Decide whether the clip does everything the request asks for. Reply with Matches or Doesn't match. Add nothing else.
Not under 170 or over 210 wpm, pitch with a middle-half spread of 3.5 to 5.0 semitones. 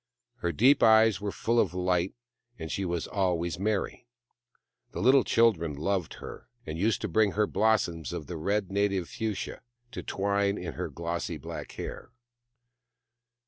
Doesn't match